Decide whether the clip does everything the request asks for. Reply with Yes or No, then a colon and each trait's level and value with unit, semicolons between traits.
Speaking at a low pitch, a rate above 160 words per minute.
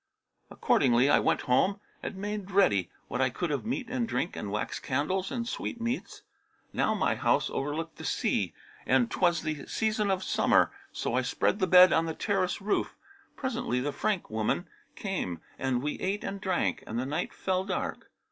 No: medium, 185 Hz; average, 180 wpm